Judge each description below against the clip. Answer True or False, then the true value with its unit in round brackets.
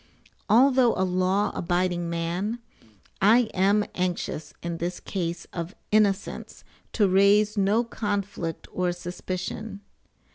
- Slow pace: True (110 wpm)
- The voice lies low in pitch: False (190 Hz)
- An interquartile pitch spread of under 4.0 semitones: True (2.9 semitones)